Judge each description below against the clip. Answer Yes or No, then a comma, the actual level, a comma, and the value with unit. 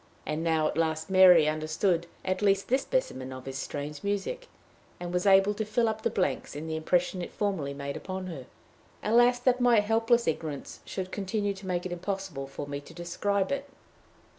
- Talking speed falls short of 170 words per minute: No, average, 190 wpm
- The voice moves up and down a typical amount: Yes, average, 4.7 semitones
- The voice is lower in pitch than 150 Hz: No, medium, 185 Hz